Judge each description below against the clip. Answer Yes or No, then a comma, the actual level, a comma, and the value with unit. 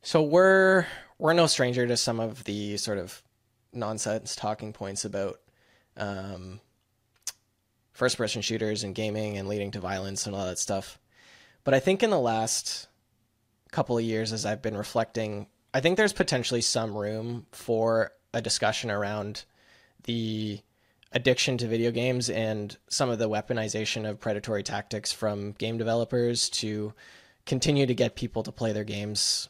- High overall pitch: No, low, 110 Hz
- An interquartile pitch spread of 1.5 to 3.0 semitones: Yes, narrow, 2.6 semitones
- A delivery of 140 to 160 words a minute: Yes, average, 155 wpm